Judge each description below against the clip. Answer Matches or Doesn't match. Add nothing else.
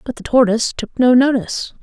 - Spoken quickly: Doesn't match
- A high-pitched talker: Matches